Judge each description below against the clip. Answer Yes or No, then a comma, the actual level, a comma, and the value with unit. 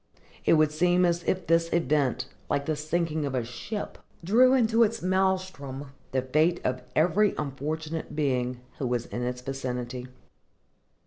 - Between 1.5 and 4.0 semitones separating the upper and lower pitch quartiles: No, average, 5.3 semitones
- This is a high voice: No, medium, 155 Hz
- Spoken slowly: No, average, 150 wpm